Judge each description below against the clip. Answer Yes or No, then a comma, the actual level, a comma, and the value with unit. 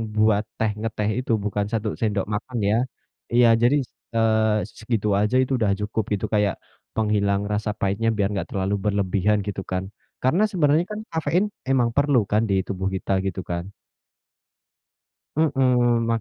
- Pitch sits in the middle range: No, low, 110 Hz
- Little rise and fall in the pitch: No, average, 3.3 semitones